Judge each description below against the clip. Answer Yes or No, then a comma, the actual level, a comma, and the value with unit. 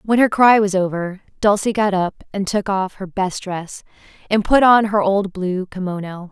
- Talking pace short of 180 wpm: No, average, 200 wpm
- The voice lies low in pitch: No, high, 195 Hz